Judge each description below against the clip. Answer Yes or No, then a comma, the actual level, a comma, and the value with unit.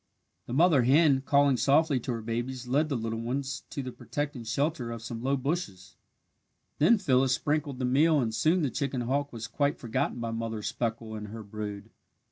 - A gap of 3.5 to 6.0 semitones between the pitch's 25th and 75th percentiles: Yes, average, 3.8 semitones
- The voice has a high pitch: No, low, 130 Hz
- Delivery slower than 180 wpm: No, average, 190 wpm